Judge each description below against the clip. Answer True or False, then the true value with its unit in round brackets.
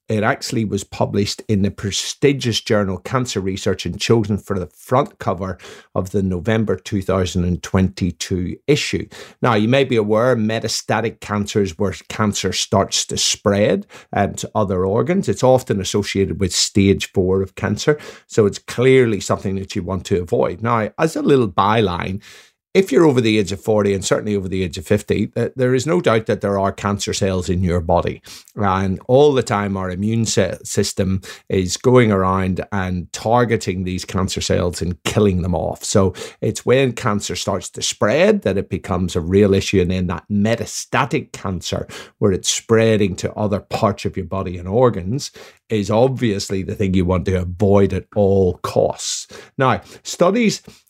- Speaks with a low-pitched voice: True (100 Hz)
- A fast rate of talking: False (175 wpm)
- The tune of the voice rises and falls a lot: False (2.8 semitones)